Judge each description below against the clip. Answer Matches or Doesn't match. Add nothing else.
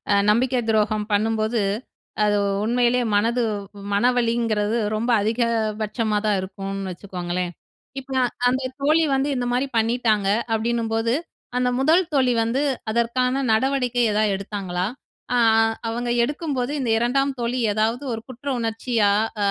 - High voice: Matches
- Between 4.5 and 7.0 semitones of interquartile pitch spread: Doesn't match